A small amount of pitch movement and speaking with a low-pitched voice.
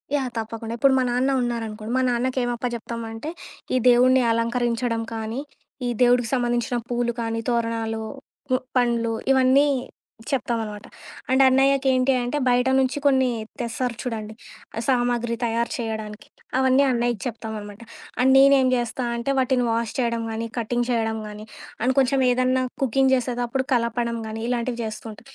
No: narrow, 2.1 semitones; high, 240 Hz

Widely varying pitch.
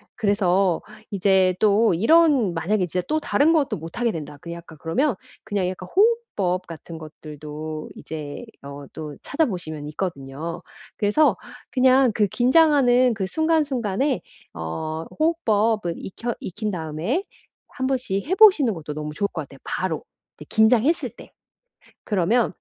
Yes: wide, 7.8 semitones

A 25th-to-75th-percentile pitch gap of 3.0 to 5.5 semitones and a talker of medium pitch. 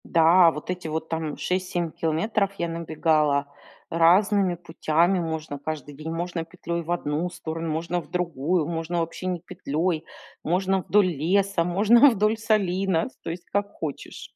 No: narrow, 2.5 semitones; medium, 170 Hz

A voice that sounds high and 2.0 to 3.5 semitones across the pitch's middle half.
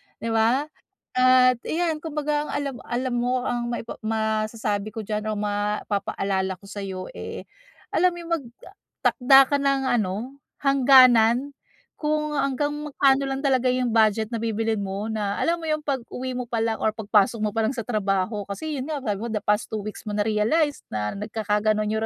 No: high, 230 Hz; average, 4.4 semitones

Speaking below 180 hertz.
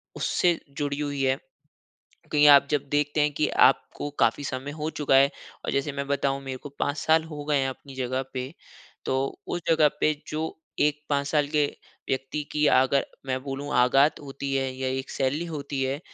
Yes: medium, 140 Hz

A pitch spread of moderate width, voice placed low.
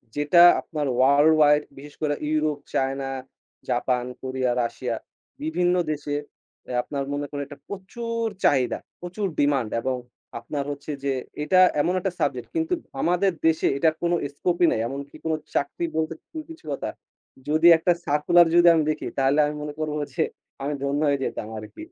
No: average, 3.8 semitones; medium, 150 Hz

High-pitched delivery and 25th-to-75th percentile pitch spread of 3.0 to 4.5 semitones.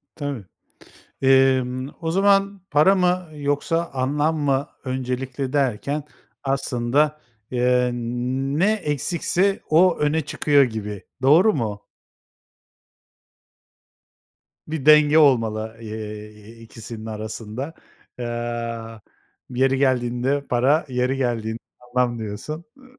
No: low, 130 Hz; average, 4.0 semitones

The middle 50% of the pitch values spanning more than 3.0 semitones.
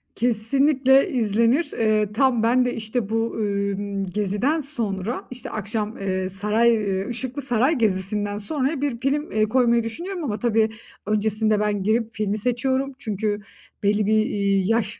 Yes: average, 3.4 semitones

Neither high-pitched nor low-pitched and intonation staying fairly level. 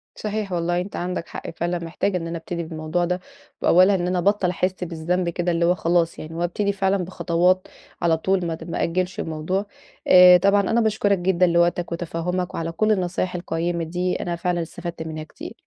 Yes: medium, 175 Hz; narrow, 1.6 semitones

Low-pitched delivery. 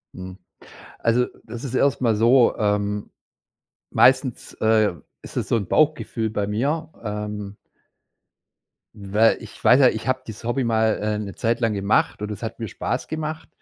Yes: low, 110 Hz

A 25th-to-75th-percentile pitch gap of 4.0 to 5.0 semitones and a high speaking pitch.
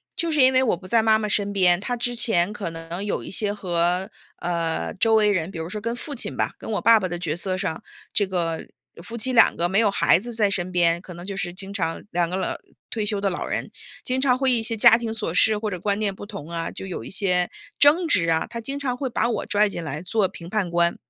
Yes: average, 4.4 semitones; high, 200 Hz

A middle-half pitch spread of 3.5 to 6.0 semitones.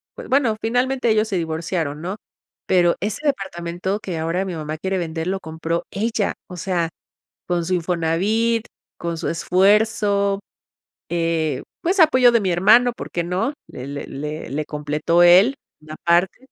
Yes: average, 4.5 semitones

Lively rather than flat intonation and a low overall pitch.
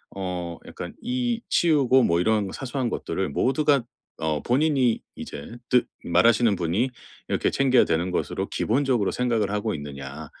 Yes: wide, 6.8 semitones; low, 115 Hz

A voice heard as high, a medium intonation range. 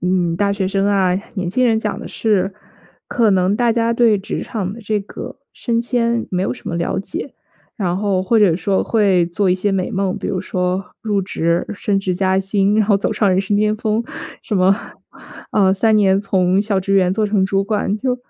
No: high, 195 Hz; narrow, 2.3 semitones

